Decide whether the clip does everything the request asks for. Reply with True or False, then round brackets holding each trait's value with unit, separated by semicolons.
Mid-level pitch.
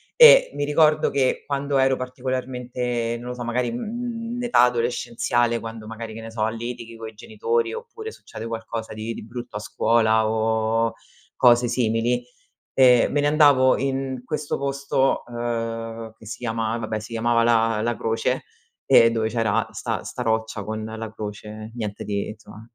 False (115 Hz)